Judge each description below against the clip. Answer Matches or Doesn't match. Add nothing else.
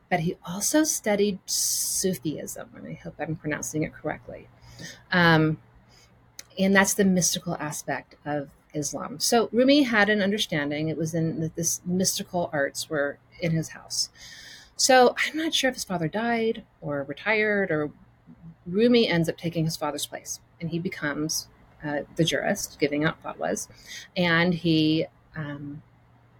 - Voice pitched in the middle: Matches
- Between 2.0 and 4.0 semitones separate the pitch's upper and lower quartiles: Doesn't match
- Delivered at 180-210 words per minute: Doesn't match